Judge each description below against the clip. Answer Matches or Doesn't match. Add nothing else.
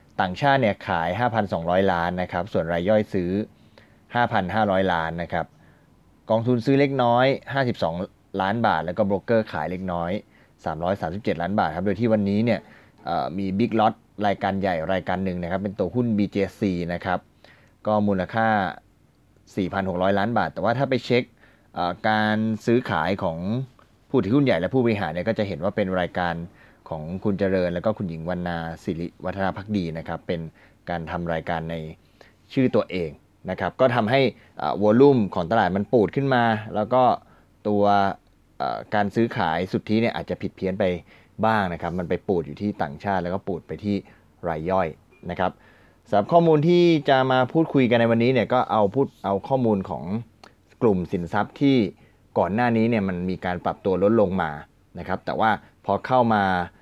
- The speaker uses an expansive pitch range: Doesn't match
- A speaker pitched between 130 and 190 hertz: Doesn't match